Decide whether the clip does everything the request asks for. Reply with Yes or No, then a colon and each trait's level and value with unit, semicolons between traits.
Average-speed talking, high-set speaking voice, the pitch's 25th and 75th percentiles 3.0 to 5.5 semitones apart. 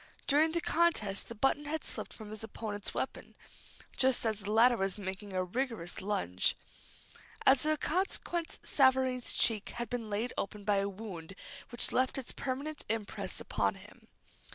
Yes: average, 160 wpm; high, 225 Hz; average, 4.7 semitones